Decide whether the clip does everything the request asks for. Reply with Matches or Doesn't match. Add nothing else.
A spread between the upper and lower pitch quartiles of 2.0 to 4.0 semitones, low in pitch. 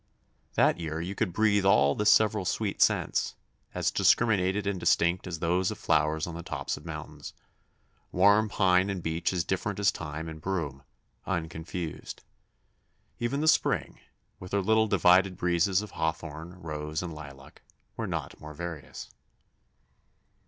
Matches